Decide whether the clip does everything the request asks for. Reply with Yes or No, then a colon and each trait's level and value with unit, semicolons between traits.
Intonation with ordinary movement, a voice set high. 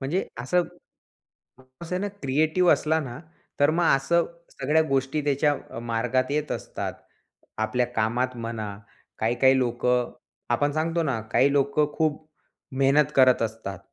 No: average, 4.0 semitones; low, 135 Hz